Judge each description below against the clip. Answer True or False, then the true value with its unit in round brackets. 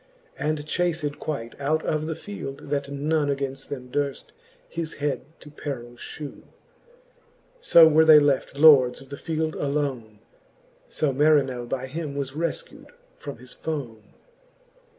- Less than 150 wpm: True (140 wpm)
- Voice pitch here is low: False (145 Hz)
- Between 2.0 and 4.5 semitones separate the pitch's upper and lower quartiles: True (2.5 semitones)